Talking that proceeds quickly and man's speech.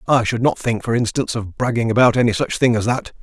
Yes: fast, 260 wpm; male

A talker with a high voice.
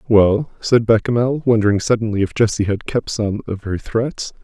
No: low, 110 Hz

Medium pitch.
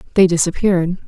Yes: medium, 180 Hz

